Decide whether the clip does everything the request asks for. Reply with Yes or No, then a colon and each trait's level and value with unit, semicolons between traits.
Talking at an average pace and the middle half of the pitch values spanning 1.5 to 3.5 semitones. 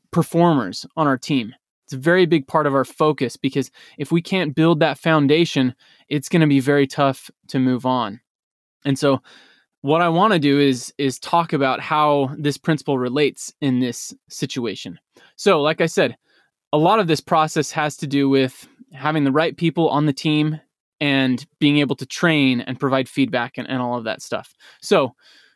Yes: average, 190 wpm; average, 3.2 semitones